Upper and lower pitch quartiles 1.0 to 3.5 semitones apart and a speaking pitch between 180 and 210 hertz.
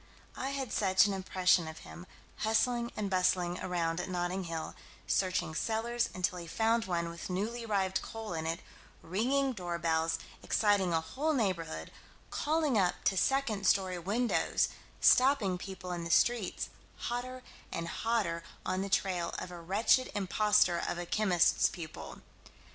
No: average, 4.3 semitones; high, 190 Hz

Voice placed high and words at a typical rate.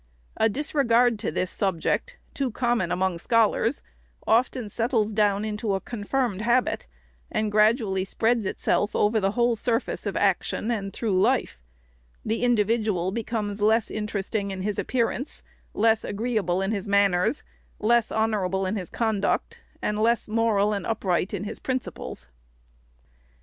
Yes: high, 215 Hz; average, 145 wpm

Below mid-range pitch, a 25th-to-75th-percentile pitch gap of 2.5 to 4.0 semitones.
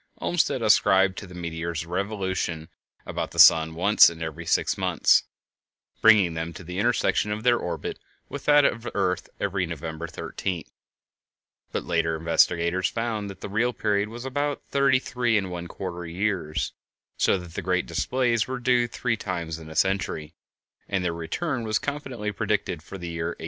No: very low, 95 Hz; average, 5.2 semitones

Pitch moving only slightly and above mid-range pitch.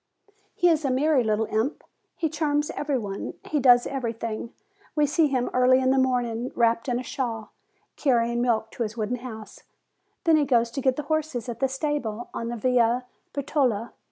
No: average, 3.4 semitones; very high, 250 Hz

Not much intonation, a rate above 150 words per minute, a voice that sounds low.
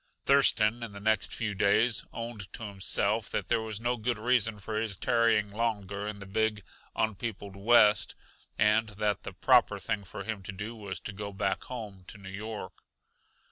Yes: narrow, 2.1 semitones; average, 180 wpm; low, 105 Hz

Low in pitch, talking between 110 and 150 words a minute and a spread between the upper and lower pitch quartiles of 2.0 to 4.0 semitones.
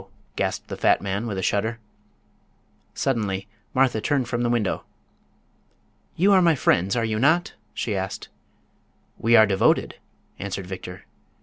No: low, 110 Hz; average, 140 wpm; average, 4.5 semitones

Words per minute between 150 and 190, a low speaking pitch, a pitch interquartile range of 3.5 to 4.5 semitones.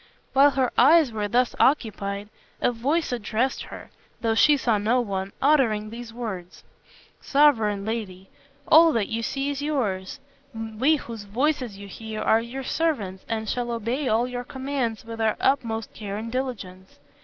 No: average, 160 wpm; high, 230 Hz; average, 3.9 semitones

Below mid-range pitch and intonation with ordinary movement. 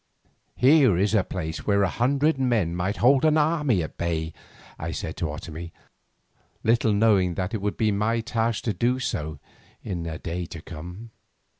No: low, 100 Hz; wide, 5.8 semitones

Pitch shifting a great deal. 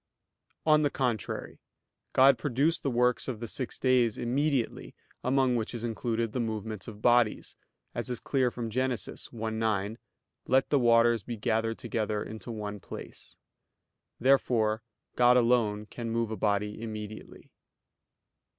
No: narrow, 2.4 semitones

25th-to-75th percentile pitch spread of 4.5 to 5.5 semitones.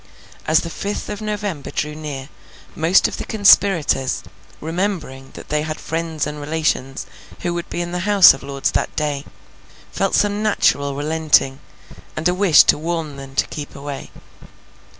No: average, 3.7 semitones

